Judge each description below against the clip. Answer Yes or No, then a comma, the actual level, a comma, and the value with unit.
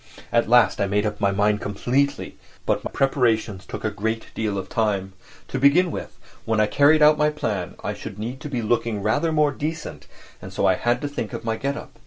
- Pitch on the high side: No, low, 115 Hz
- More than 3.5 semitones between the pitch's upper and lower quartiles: Yes, average, 5.3 semitones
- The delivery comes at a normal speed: No, fast, 225 wpm